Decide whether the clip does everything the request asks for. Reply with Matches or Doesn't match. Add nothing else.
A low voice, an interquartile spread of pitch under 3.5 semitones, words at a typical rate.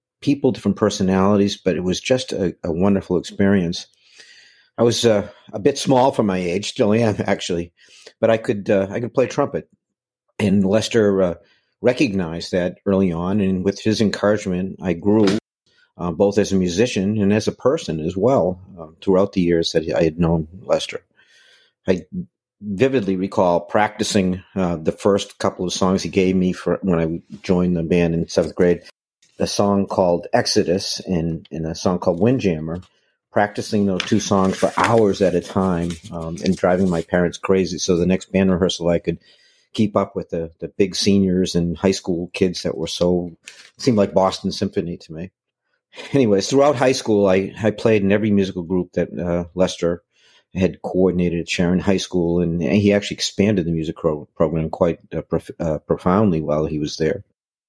Matches